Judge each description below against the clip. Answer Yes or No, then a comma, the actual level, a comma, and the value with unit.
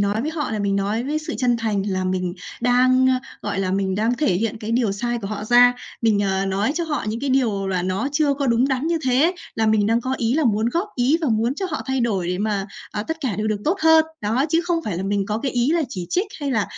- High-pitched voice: Yes, high, 230 Hz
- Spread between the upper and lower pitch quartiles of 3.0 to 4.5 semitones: No, average, 5.0 semitones